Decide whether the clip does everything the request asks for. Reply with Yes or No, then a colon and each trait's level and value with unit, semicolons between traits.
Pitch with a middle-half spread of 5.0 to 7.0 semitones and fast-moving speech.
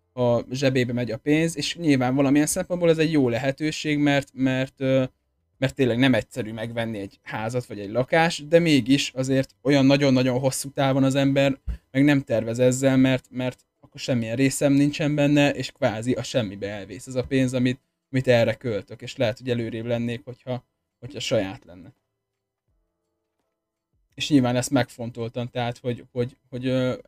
No: narrow, 2.5 semitones; fast, 165 wpm